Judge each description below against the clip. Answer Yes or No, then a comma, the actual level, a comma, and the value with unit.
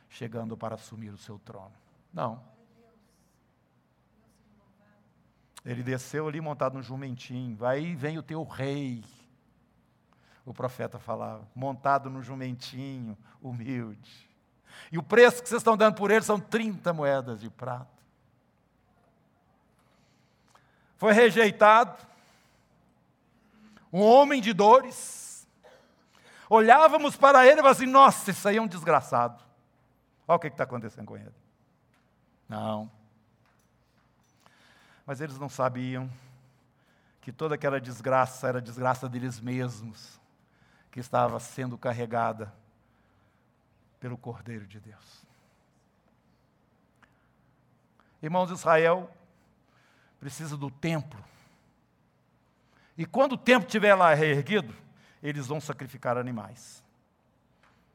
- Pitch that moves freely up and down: Yes, wide, 5.7 semitones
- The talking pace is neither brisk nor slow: No, slow, 105 wpm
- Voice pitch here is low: Yes, low, 130 Hz